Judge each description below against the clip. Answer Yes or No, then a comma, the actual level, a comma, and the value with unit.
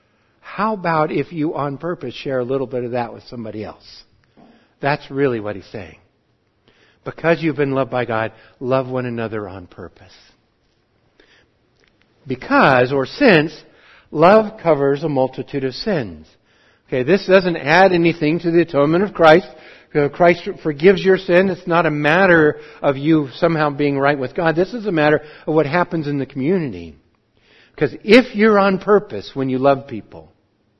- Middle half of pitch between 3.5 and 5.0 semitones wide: No, wide, 5.6 semitones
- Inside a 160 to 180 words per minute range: Yes, average, 165 wpm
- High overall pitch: No, medium, 145 Hz